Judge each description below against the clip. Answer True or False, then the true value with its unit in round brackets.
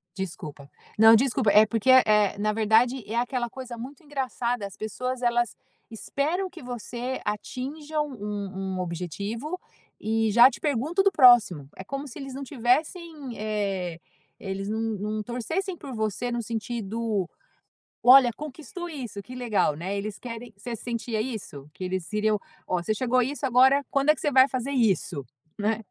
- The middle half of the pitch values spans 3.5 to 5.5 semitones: True (3.9 semitones)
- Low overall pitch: False (235 Hz)